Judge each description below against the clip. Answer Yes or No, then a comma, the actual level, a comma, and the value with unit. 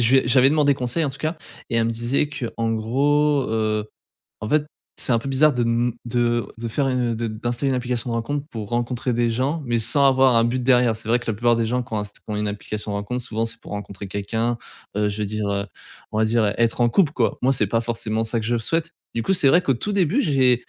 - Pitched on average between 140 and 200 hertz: No, low, 120 Hz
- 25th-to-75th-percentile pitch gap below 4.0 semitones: Yes, average, 3.0 semitones